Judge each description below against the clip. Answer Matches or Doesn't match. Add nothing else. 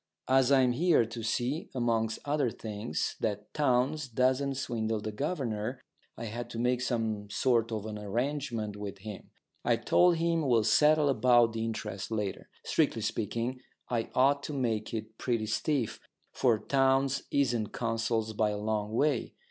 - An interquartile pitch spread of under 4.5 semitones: Matches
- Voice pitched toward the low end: Matches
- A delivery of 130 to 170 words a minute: Matches